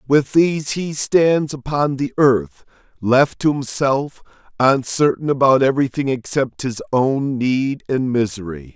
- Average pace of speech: No, slow, 130 wpm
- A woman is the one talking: No, male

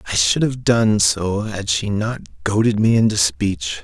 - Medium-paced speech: Yes, average, 190 wpm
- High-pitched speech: No, low, 105 Hz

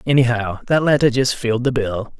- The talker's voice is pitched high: No, low, 125 Hz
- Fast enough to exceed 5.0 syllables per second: Yes, 5.5 syllables/s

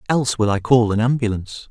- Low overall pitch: Yes, low, 115 Hz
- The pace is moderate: No, fast, 210 wpm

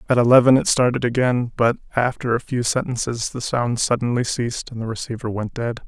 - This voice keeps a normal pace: Yes, average, 195 wpm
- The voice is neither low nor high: No, low, 120 Hz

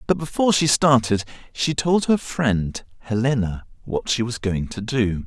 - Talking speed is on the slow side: No, average, 170 wpm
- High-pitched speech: No, low, 120 Hz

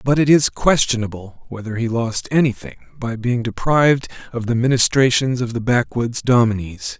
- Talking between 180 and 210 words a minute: No, average, 155 wpm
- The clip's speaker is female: No, male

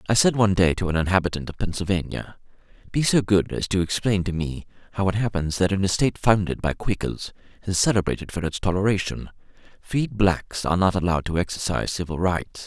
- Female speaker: No, male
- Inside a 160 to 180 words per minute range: No, average, 195 wpm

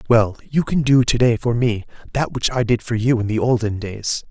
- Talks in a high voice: No, low, 120 Hz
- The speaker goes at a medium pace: No, fast, 250 wpm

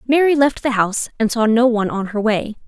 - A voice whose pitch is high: Yes, high, 235 Hz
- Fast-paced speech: Yes, fast, 245 wpm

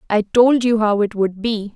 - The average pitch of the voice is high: Yes, high, 215 Hz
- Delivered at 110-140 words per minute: No, fast, 240 wpm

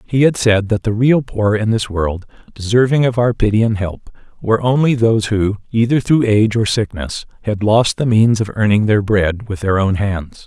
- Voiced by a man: Yes, male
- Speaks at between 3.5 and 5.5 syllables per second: Yes, 5.0 syllables/s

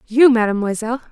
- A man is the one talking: No, female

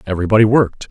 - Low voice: Yes, low, 105 Hz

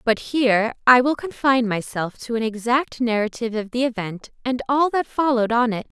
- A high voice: Yes, high, 240 Hz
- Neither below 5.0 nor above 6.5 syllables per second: Yes, 5.5 syllables/s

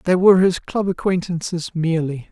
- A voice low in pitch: No, medium, 175 Hz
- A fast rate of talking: No, average, 155 wpm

